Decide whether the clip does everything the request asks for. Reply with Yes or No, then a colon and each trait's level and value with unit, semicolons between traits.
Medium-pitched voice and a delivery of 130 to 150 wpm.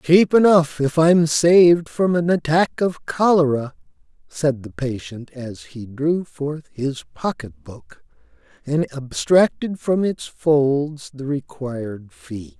Yes: medium, 150 Hz; average, 140 wpm